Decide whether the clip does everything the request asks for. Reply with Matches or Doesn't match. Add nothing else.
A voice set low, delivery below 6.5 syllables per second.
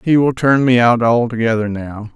Matches